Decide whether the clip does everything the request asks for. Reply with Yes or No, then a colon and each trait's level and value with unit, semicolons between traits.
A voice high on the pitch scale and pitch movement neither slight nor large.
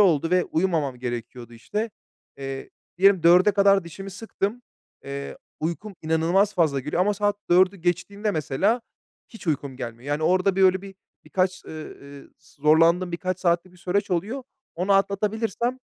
No: medium, 180 Hz; average, 4.1 semitones